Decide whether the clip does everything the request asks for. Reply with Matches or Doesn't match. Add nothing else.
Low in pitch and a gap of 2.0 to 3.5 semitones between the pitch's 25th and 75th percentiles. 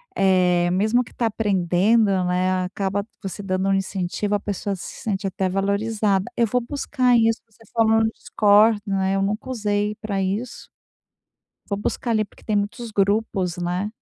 Doesn't match